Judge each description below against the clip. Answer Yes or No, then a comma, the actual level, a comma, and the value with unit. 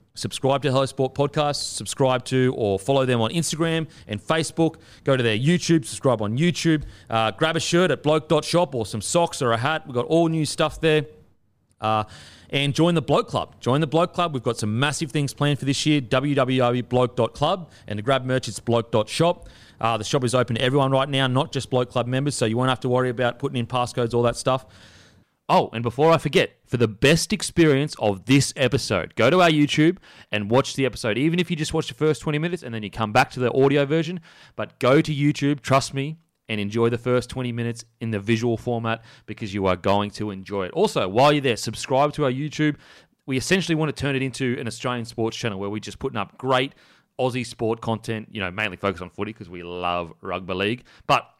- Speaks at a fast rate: Yes, fast, 225 wpm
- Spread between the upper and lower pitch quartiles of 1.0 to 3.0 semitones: No, average, 4.8 semitones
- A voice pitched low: Yes, low, 130 Hz